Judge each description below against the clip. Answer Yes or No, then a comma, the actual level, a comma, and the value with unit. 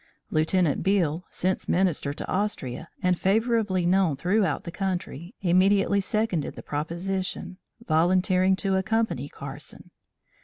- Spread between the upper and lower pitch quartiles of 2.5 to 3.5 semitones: Yes, average, 2.9 semitones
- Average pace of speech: No, slow, 115 wpm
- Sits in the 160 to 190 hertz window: Yes, medium, 185 Hz